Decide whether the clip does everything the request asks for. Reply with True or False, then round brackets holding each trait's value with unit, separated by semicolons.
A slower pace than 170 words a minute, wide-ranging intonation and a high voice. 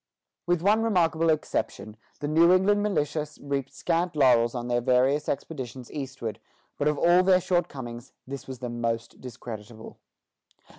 False (145 wpm; 5.7 semitones; 140 Hz)